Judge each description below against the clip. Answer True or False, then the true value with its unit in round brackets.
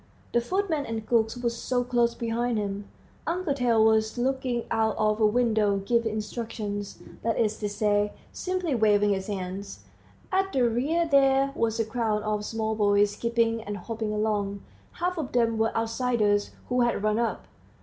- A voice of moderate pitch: False (225 Hz)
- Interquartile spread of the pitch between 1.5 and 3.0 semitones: True (2.6 semitones)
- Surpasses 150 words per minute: True (165 wpm)